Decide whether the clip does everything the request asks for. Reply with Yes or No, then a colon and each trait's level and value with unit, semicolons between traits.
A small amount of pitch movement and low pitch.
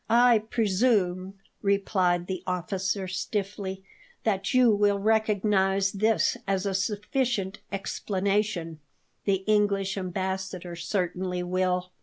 No: narrow, 2.0 semitones; high, 195 Hz